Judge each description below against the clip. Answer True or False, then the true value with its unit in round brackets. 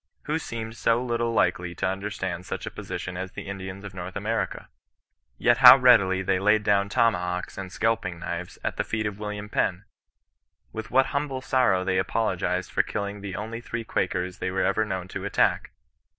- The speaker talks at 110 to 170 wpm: False (185 wpm)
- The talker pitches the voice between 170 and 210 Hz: False (100 Hz)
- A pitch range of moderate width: True (3.3 semitones)